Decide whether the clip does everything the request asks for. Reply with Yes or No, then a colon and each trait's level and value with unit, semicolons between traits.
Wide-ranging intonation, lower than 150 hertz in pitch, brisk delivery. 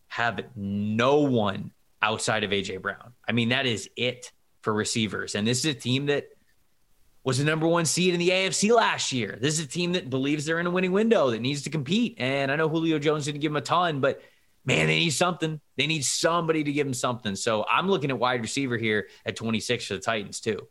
Yes: wide, 5.9 semitones; low, 135 Hz; fast, 230 wpm